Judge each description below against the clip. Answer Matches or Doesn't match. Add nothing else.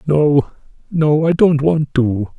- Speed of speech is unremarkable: Matches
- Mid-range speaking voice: Matches